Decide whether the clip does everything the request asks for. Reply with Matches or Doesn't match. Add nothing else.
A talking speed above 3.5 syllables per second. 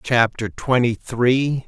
Doesn't match